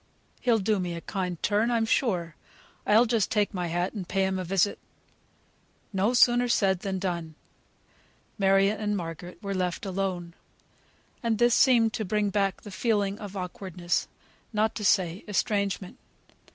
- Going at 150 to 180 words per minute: Yes, average, 155 wpm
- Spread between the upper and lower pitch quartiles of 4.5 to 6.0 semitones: No, average, 2.9 semitones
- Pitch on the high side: Yes, high, 195 Hz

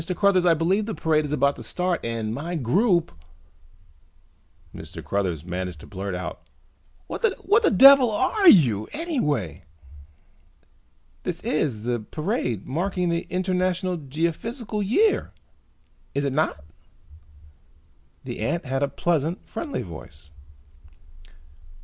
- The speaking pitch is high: No, medium, 160 Hz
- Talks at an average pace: No, slow, 120 wpm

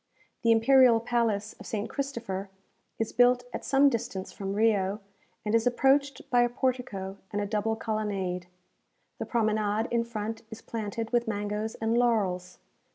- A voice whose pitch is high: Yes, high, 225 Hz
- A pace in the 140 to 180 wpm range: Yes, average, 155 wpm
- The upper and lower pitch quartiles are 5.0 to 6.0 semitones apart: No, average, 2.7 semitones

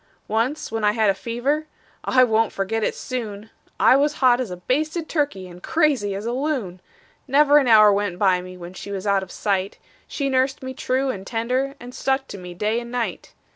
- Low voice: No, high, 230 Hz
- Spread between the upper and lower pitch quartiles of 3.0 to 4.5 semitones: No, average, 5.0 semitones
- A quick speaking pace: Yes, fast, 210 wpm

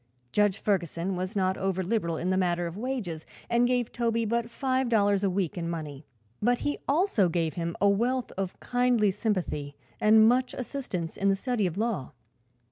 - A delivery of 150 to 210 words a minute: Yes, average, 185 wpm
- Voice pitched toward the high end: Yes, high, 200 Hz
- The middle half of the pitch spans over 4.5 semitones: Yes, average, 5.0 semitones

